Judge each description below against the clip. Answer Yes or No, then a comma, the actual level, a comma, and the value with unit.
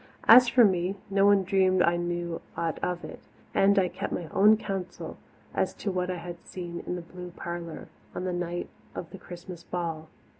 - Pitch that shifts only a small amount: Yes, narrow, 2.0 semitones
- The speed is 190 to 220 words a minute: Yes, average, 195 wpm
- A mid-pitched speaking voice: Yes, medium, 180 Hz